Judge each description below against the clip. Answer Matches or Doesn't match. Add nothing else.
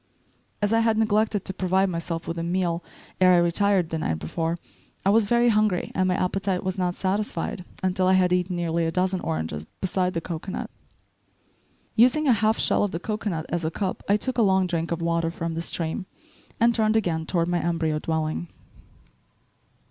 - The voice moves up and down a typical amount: Matches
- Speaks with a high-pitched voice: Doesn't match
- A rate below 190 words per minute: Doesn't match